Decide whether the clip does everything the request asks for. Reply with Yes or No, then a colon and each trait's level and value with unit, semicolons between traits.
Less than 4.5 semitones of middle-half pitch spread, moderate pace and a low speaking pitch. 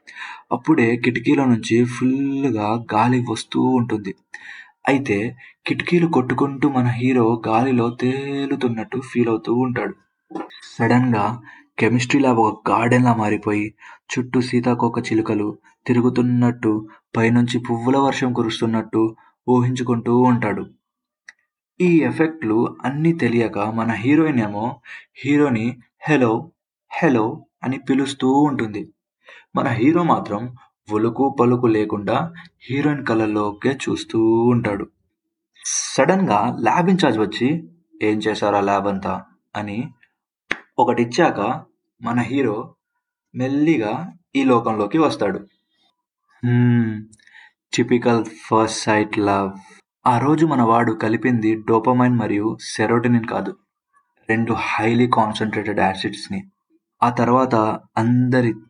Yes: average, 3.2 semitones; average, 100 wpm; low, 120 Hz